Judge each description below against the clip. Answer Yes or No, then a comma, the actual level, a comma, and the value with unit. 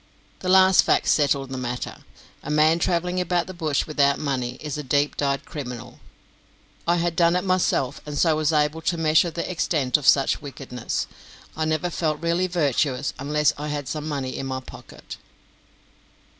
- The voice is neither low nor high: Yes, medium, 150 Hz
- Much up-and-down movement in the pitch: No, average, 3.5 semitones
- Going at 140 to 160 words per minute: No, average, 175 wpm